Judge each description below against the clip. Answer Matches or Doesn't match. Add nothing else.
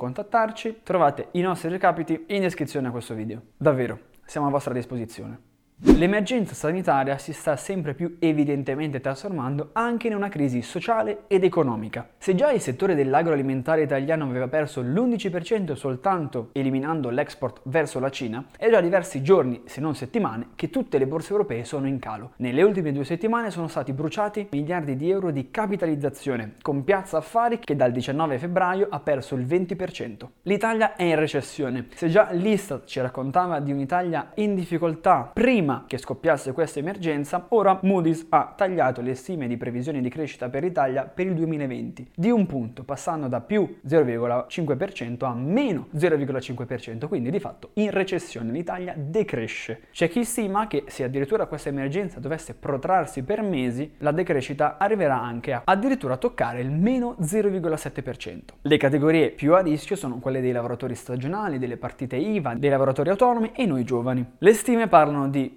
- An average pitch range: Doesn't match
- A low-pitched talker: Doesn't match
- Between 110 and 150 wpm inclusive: Doesn't match